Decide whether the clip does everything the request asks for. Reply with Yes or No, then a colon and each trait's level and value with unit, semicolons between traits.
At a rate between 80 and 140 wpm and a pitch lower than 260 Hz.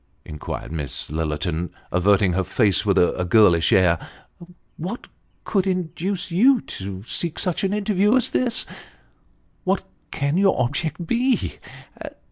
Yes: slow, 135 wpm; medium, 140 Hz